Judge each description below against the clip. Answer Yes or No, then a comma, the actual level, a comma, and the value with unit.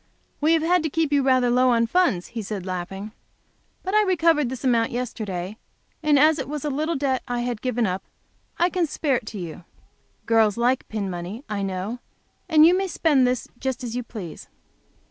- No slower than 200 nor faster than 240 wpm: Yes, fast, 205 wpm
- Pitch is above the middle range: Yes, very high, 250 Hz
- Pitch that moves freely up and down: Yes, wide, 5.9 semitones